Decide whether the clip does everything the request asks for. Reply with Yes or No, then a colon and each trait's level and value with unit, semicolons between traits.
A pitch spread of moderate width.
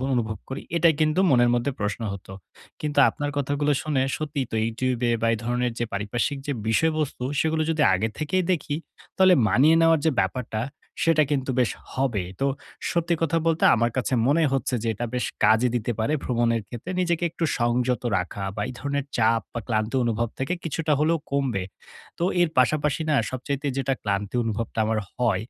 Yes: average, 4.8 semitones